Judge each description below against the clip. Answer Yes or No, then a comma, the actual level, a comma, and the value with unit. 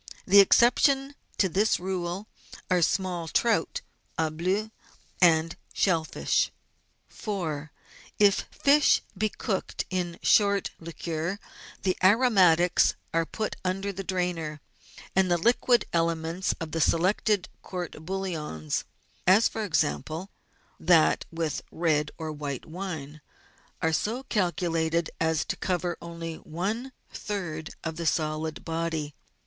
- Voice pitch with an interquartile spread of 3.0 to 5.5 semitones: Yes, average, 3.3 semitones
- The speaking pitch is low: No, medium, 175 Hz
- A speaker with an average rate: No, slow, 125 wpm